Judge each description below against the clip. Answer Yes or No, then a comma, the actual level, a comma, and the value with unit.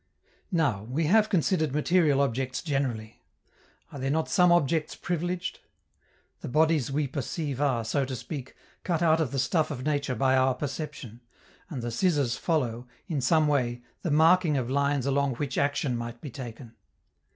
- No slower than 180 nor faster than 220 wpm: No, average, 165 wpm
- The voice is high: No, medium, 140 Hz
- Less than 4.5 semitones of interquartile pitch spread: Yes, average, 3.8 semitones